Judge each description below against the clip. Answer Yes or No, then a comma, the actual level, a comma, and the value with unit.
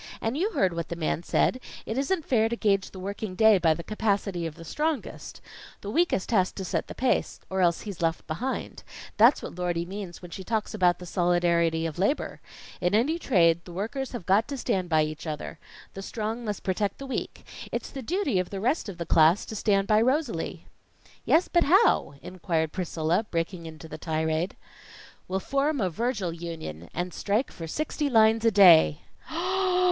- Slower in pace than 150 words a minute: No, average, 195 wpm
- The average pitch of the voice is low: No, high, 190 Hz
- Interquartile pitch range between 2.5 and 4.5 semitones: No, average, 5.1 semitones